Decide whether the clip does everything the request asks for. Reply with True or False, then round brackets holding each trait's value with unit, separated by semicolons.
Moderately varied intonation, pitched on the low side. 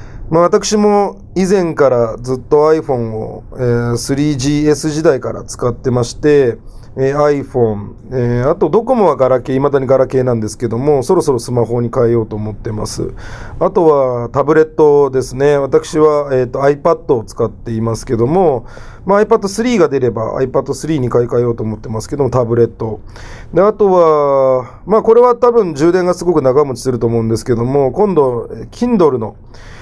True (4.7 semitones; 130 Hz)